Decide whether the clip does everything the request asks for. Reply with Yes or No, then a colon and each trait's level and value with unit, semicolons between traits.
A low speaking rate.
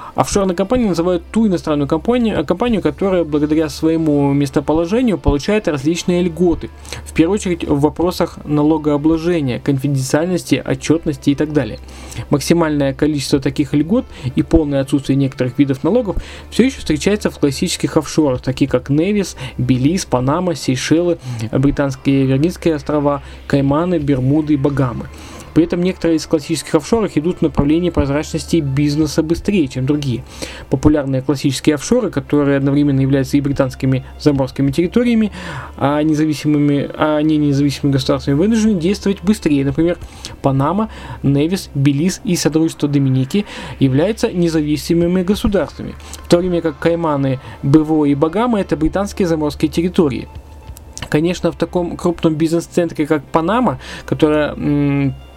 No: average, 130 wpm